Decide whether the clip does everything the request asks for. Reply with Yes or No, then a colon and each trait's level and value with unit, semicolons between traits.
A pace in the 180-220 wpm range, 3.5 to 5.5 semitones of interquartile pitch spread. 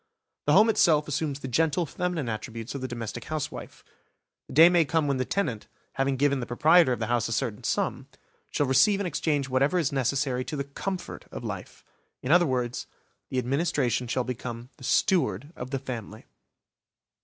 Yes: average, 185 wpm; average, 4.1 semitones